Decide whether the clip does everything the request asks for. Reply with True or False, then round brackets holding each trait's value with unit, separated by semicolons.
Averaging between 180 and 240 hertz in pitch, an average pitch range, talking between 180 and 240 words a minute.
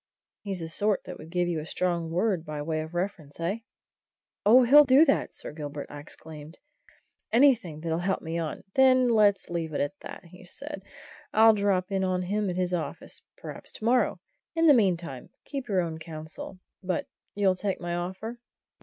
True (185 Hz; 4.5 semitones; 190 wpm)